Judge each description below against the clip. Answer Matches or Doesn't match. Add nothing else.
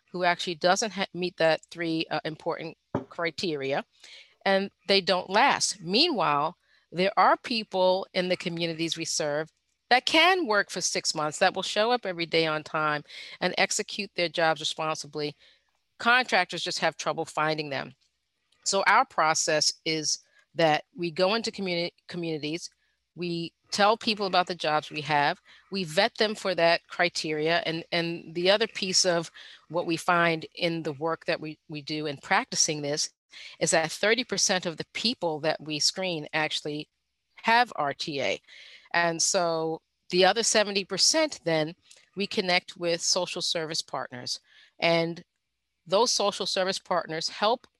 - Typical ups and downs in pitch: Matches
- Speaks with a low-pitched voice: Doesn't match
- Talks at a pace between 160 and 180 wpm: Doesn't match